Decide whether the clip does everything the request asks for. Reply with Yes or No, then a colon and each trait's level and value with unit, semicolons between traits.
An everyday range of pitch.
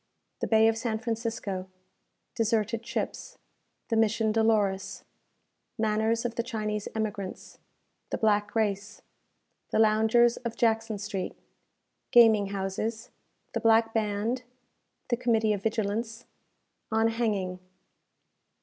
No: narrow, 1.5 semitones